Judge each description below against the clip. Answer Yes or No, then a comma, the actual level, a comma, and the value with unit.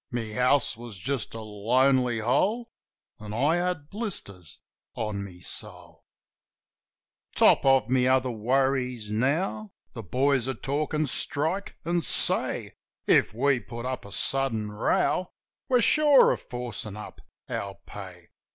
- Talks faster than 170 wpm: No, slow, 135 wpm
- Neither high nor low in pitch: No, low, 125 Hz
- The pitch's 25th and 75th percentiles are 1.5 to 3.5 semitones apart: No, average, 4.9 semitones